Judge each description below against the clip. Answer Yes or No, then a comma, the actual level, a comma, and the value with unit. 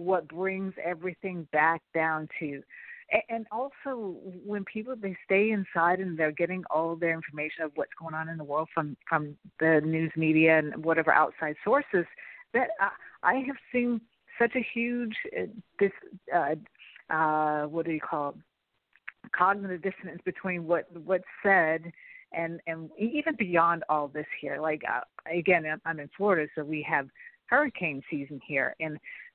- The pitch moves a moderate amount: Yes, average, 4.0 semitones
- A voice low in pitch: No, medium, 170 Hz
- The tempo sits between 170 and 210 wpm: No, average, 160 wpm